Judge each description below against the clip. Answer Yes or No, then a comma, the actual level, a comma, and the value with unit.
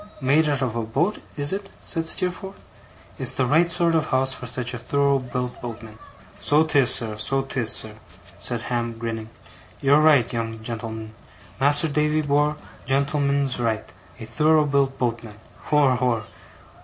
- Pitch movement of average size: Yes, average, 4.2 semitones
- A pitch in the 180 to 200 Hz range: No, low, 135 Hz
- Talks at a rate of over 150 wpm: Yes, average, 165 wpm